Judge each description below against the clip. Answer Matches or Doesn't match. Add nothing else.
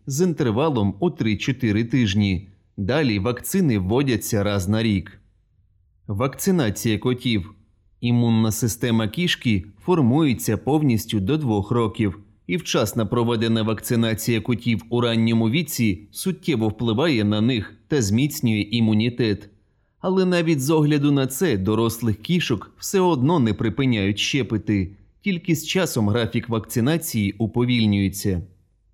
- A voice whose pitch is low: Matches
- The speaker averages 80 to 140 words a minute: Matches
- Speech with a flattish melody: Doesn't match